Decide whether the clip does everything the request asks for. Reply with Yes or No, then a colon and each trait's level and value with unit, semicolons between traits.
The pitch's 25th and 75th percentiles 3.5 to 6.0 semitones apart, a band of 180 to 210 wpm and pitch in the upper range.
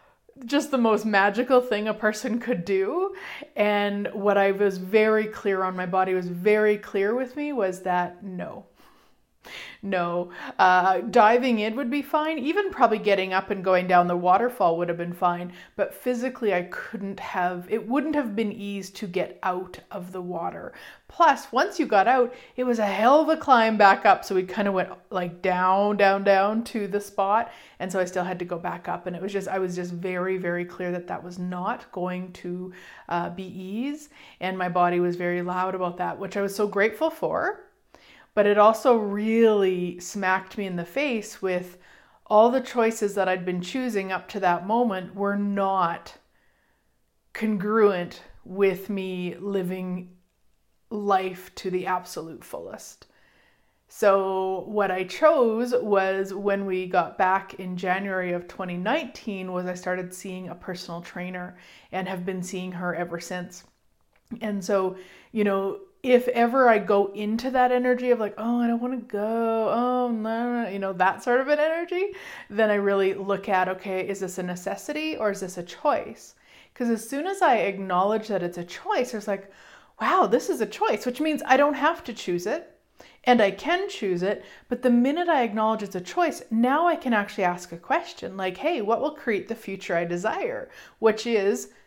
Yes: average, 4.3 semitones; average, 190 wpm; high, 200 Hz